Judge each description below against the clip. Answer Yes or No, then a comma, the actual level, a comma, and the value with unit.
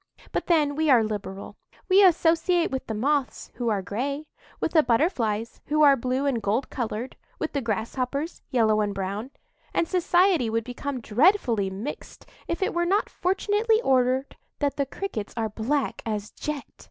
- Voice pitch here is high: Yes, very high, 265 Hz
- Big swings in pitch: Yes, wide, 6.2 semitones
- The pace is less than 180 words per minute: Yes, average, 165 wpm